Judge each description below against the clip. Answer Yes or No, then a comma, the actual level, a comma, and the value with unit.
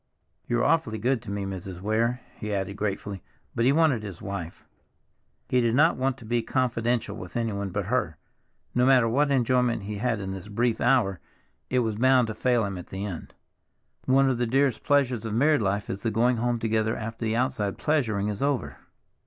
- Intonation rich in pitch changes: No, average, 3.7 semitones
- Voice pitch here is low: Yes, low, 115 Hz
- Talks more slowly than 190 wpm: No, average, 195 wpm